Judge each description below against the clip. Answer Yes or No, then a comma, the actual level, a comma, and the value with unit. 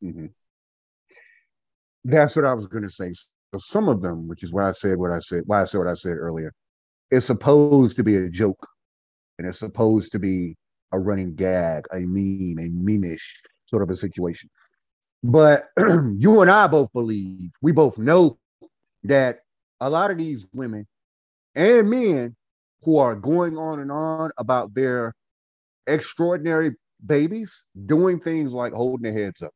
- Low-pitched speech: Yes, low, 110 Hz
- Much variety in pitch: Yes, wide, 8.4 semitones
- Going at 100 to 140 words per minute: No, average, 165 wpm